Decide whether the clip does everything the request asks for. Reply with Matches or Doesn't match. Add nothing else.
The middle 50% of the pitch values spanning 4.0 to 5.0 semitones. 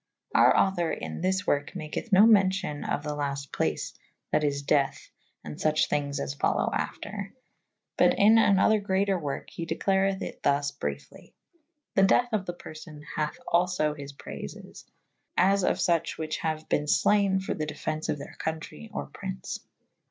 Matches